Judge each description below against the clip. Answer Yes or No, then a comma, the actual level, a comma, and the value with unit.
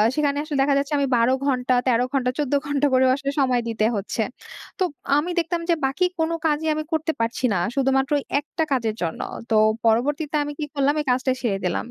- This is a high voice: Yes, very high, 275 Hz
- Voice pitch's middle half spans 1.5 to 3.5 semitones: Yes, average, 3.1 semitones